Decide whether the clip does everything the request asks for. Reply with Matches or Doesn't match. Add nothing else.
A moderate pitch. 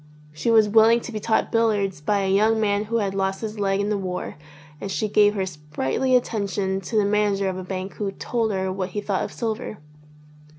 Doesn't match